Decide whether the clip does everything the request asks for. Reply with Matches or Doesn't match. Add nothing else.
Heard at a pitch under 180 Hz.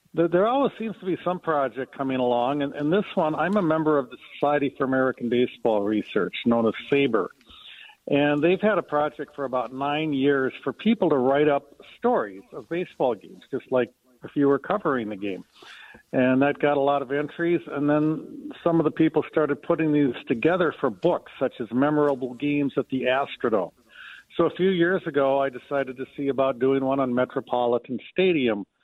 Matches